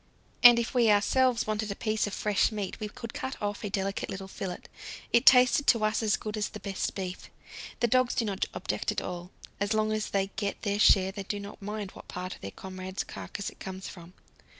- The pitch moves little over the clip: Yes, narrow, 2.1 semitones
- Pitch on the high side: Yes, high, 205 Hz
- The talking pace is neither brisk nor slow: No, fast, 225 wpm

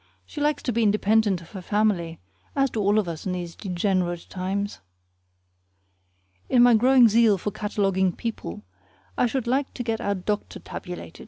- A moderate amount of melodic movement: Yes, average, 4.1 semitones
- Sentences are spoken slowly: No, average, 170 wpm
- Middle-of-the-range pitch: No, high, 205 Hz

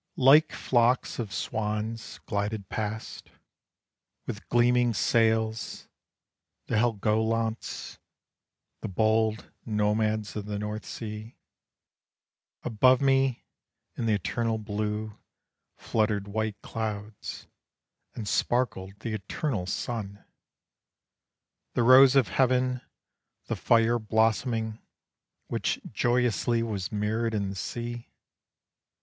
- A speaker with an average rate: No, slow, 95 wpm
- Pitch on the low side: Yes, low, 110 Hz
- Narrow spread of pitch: Yes, narrow, 2.1 semitones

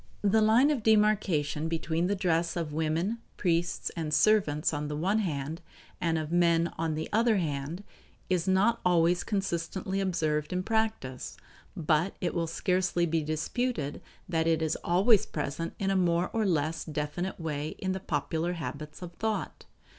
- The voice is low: No, medium, 170 Hz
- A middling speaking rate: Yes, average, 160 wpm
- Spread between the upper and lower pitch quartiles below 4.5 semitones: Yes, average, 3.6 semitones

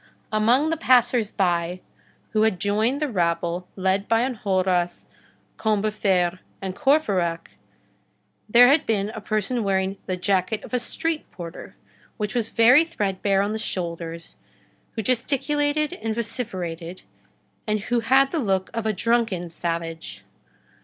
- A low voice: No, high, 210 Hz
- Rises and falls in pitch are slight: No, average, 4.7 semitones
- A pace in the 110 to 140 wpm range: Yes, slow, 135 wpm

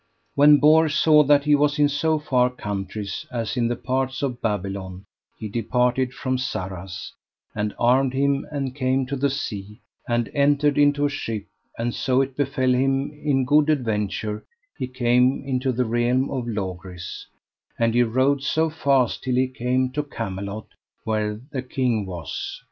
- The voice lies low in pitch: Yes, low, 130 Hz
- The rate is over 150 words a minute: Yes, average, 165 wpm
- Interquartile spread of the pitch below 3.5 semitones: No, average, 4.0 semitones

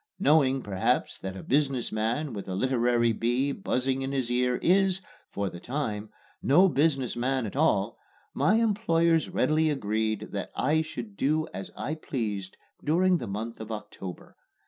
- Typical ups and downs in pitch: No, wide, 6.0 semitones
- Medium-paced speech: Yes, average, 160 wpm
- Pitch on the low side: Yes, low, 130 Hz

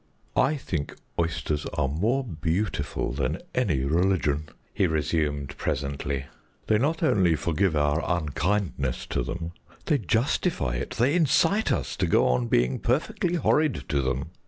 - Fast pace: No, average, 140 wpm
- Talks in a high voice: No, very low, 80 Hz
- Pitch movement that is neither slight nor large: No, wide, 8.4 semitones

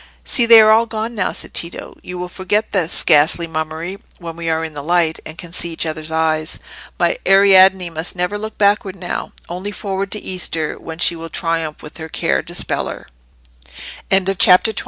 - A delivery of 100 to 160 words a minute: No, average, 185 wpm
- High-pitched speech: No, medium, 180 Hz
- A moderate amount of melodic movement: Yes, average, 3.3 semitones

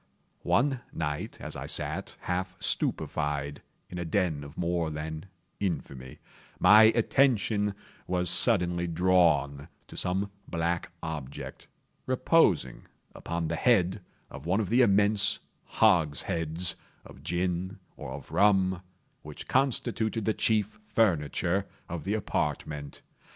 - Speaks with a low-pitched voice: Yes, very low, 90 Hz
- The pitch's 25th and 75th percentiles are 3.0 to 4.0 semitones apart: No, average, 4.6 semitones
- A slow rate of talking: Yes, slow, 120 wpm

